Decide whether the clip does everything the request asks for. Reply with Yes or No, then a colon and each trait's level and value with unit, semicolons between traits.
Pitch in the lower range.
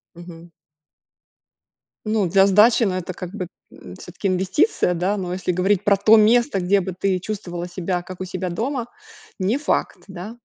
No: high, 190 Hz